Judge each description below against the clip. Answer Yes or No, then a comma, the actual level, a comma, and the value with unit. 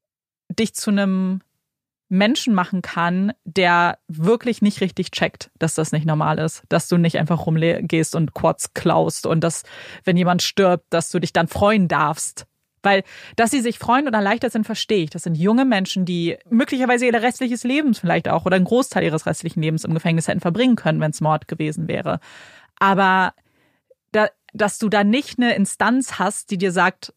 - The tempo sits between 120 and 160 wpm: No, average, 185 wpm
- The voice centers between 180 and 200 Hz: Yes, medium, 185 Hz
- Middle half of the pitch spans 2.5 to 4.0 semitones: No, average, 4.6 semitones